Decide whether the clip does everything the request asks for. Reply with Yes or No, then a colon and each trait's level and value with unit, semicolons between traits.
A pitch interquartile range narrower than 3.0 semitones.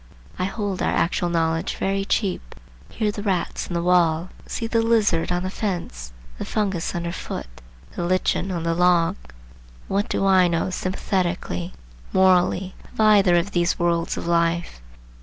Yes: narrow, 2.4 semitones